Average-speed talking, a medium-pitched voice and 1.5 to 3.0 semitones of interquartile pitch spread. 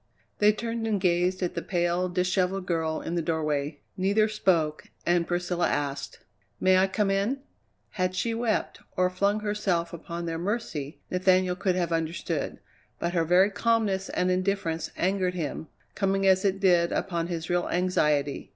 Yes: average, 160 wpm; medium, 180 Hz; narrow, 2.4 semitones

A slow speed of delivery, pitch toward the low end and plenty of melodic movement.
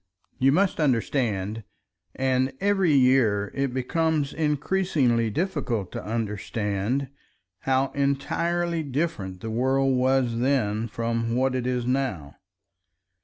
No: slow, 100 wpm; low, 130 Hz; average, 3.6 semitones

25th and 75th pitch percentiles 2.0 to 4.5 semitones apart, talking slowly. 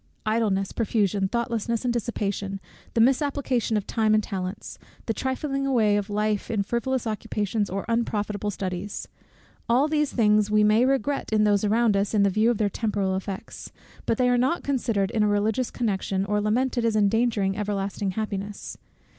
No: average, 2.8 semitones; average, 170 wpm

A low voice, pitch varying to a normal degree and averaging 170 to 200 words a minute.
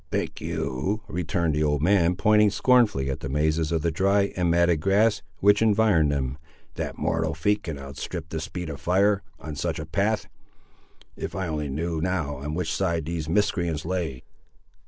Yes: very low, 85 Hz; average, 4.4 semitones; average, 180 wpm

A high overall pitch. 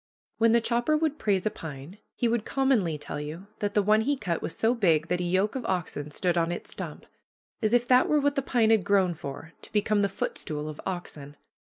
Yes: high, 200 Hz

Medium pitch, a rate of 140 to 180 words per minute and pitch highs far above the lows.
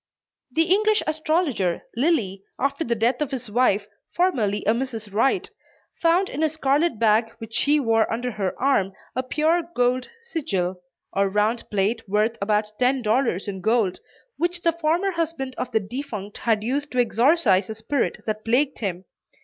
No: high, 245 Hz; average, 165 wpm; wide, 6.1 semitones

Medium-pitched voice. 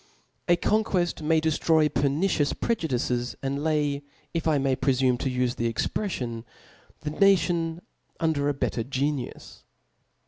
Yes: medium, 145 Hz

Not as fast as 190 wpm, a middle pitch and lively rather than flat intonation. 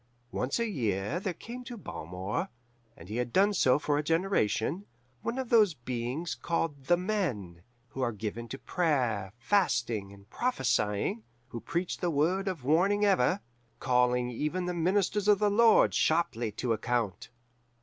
Yes: average, 160 wpm; medium, 150 Hz; wide, 8.5 semitones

